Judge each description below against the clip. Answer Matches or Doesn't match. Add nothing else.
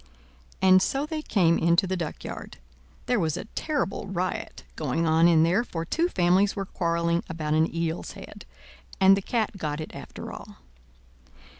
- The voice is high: Doesn't match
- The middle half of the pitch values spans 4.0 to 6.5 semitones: Doesn't match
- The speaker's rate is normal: Matches